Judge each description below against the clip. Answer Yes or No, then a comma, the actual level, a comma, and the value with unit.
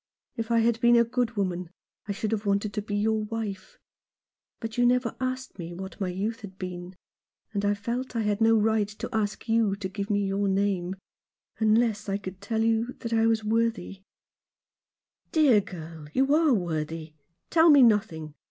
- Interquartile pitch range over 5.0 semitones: No, average, 2.8 semitones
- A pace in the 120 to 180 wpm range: No, average, 190 wpm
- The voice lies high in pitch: Yes, high, 215 Hz